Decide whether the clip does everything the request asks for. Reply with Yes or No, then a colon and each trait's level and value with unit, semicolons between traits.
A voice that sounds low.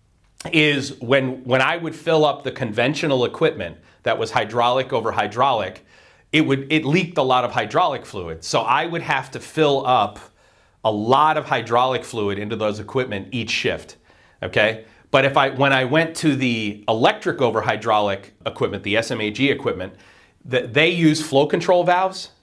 Yes: low, 130 Hz